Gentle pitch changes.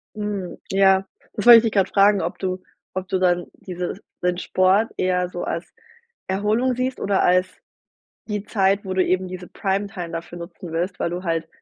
Yes: narrow, 2.0 semitones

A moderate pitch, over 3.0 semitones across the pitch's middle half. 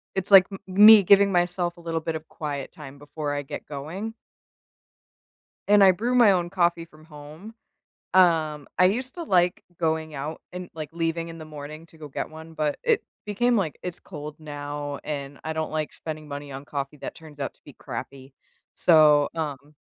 Yes: medium, 160 Hz; average, 3.5 semitones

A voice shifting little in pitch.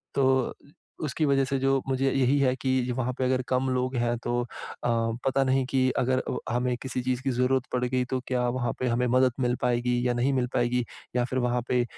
Yes: narrow, 1.2 semitones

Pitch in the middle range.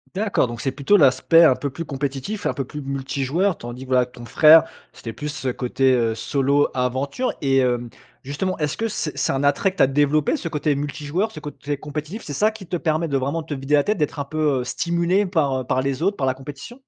Yes: medium, 145 Hz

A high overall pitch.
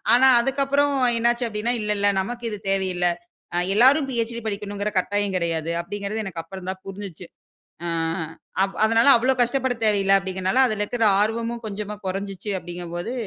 Yes: high, 205 Hz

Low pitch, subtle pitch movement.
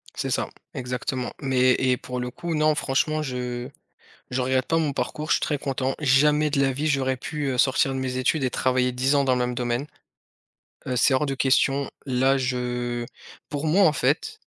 Yes: low, 130 Hz; narrow, 2.3 semitones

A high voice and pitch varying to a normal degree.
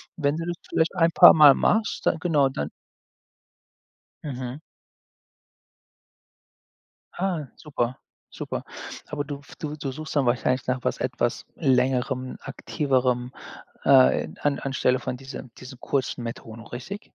No: low, 135 Hz; average, 3.1 semitones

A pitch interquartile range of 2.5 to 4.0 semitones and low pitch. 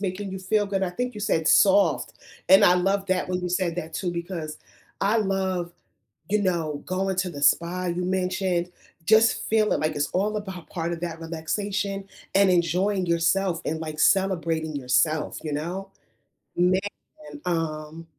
No: average, 2.8 semitones; medium, 180 Hz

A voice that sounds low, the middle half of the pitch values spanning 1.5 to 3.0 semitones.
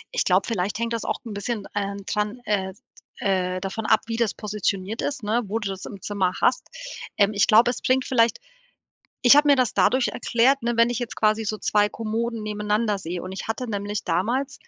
No: high, 215 Hz; average, 2.7 semitones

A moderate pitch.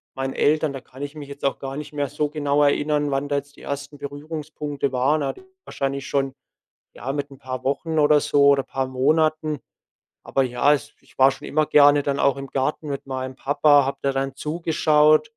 Yes: medium, 145 Hz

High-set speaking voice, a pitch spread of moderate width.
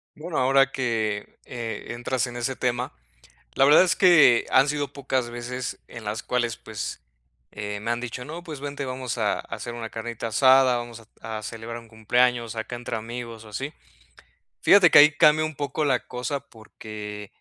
No: low, 120 Hz; average, 3.2 semitones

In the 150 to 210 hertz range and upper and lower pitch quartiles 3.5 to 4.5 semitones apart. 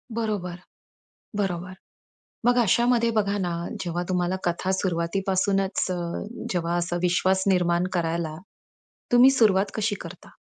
No: medium, 185 Hz; average, 2.7 semitones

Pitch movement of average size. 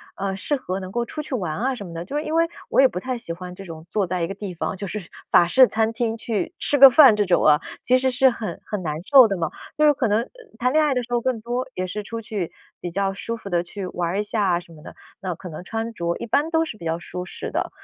No: wide, 5.7 semitones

